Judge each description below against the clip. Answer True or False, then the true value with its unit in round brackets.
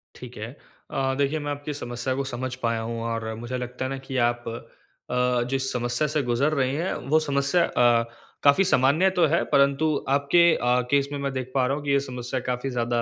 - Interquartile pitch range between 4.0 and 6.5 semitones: False (2.7 semitones)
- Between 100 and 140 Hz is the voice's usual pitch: True (135 Hz)